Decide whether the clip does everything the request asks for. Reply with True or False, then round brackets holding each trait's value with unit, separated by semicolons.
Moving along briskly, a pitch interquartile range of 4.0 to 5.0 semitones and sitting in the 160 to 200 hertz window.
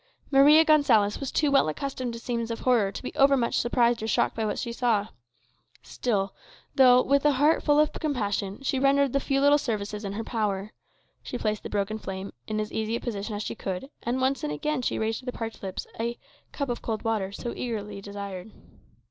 False (215 wpm; 4.7 semitones; 230 Hz)